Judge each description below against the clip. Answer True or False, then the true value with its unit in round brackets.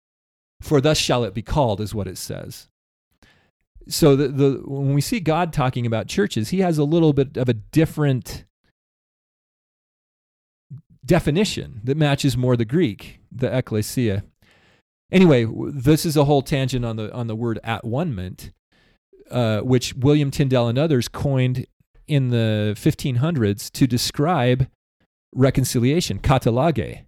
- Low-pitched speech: True (130 Hz)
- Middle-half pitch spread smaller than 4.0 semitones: False (4.8 semitones)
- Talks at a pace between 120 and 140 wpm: True (135 wpm)